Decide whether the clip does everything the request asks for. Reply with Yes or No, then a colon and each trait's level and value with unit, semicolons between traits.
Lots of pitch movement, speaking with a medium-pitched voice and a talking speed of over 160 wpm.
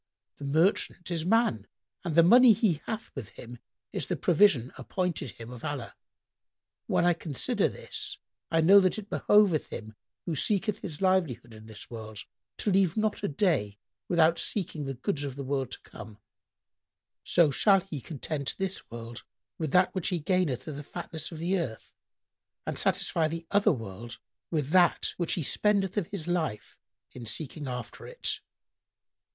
Yes: wide, 6.4 semitones; medium, 160 Hz; average, 170 wpm